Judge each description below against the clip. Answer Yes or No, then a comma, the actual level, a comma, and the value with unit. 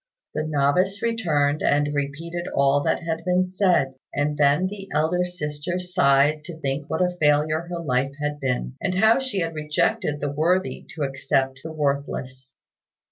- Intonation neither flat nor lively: Yes, average, 3.9 semitones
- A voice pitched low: No, medium, 150 Hz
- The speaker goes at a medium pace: Yes, average, 165 wpm